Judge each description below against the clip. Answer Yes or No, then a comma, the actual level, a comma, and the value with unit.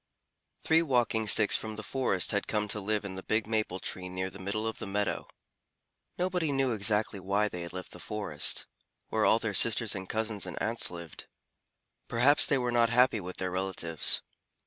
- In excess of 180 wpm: Yes, average, 190 wpm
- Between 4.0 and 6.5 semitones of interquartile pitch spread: No, average, 3.6 semitones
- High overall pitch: No, low, 105 Hz